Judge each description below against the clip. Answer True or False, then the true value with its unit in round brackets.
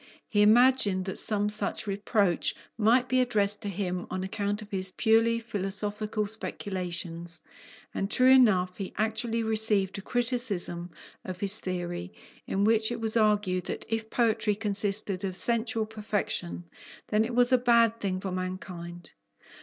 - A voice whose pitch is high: True (210 Hz)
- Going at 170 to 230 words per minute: False (150 wpm)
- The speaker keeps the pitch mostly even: False (3.1 semitones)